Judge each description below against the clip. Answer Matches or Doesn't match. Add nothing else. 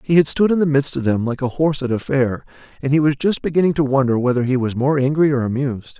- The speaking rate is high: Matches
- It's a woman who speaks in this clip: Doesn't match